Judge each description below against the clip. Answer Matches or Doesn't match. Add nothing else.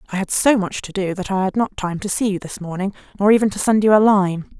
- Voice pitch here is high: Matches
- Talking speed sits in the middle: Doesn't match